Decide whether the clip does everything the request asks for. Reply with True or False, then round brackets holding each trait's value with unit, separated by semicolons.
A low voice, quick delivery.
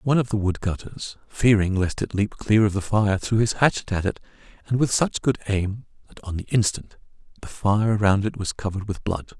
True (105 Hz; 215 wpm)